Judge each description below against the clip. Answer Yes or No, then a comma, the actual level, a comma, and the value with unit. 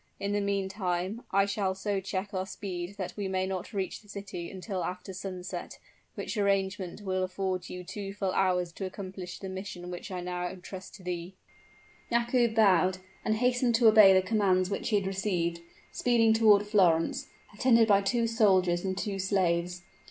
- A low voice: No, high, 190 Hz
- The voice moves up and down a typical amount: No, narrow, 2.1 semitones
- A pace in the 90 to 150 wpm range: No, average, 175 wpm